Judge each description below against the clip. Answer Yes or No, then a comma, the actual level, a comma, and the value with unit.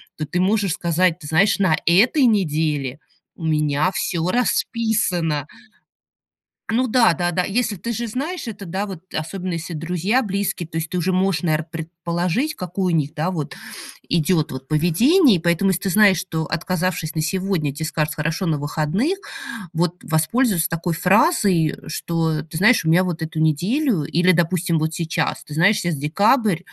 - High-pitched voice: No, medium, 175 Hz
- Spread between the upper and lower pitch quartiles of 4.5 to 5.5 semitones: No, average, 3.8 semitones